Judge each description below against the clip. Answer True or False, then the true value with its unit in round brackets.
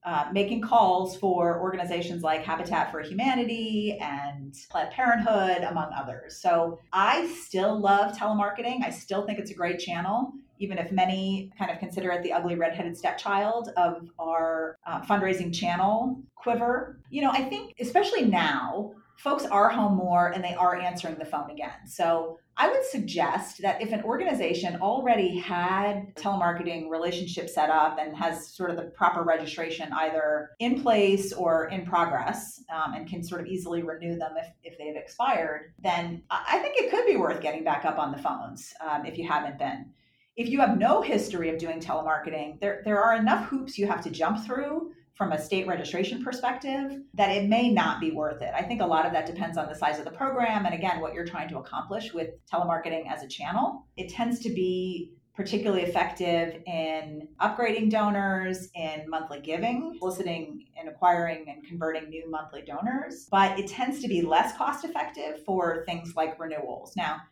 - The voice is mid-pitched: True (180 Hz)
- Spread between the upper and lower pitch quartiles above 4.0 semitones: True (4.7 semitones)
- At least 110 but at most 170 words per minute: False (185 wpm)